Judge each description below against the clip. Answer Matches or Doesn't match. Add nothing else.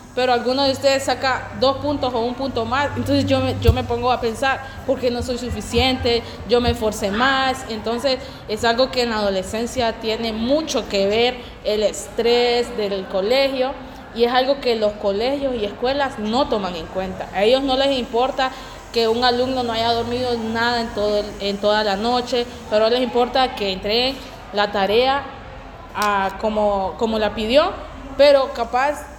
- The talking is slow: Doesn't match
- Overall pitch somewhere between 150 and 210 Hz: Doesn't match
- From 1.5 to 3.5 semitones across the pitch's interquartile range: Matches